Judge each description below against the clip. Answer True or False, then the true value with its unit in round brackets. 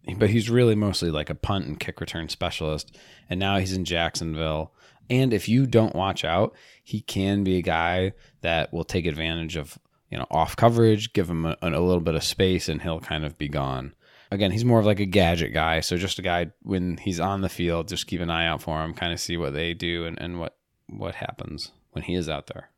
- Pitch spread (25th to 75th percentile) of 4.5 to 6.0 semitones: False (3.3 semitones)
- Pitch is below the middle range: True (85 Hz)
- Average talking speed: False (235 wpm)